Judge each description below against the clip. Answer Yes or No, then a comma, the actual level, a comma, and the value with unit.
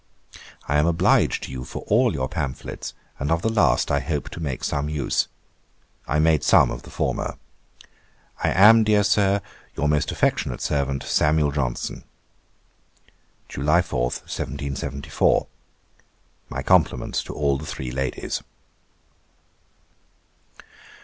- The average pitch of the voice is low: Yes, very low, 75 Hz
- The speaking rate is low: Yes, slow, 130 wpm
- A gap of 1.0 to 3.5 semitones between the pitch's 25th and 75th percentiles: No, average, 3.9 semitones